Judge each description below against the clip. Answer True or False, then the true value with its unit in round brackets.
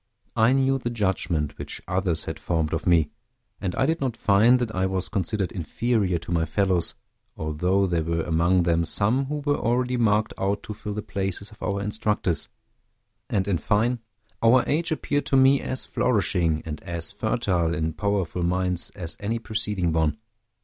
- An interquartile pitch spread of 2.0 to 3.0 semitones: False (4.9 semitones)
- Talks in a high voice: False (100 Hz)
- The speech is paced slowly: False (175 wpm)